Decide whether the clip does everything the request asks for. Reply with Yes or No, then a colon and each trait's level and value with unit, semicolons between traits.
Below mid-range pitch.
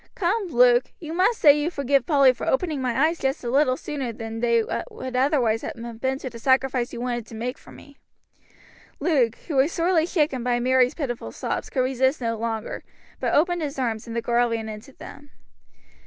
No: very high, 260 Hz